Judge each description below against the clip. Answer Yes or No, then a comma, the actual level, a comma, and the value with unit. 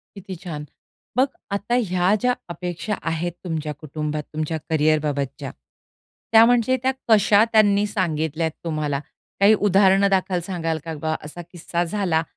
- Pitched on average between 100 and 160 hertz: No, medium, 175 Hz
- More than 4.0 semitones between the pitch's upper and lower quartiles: Yes, average, 4.4 semitones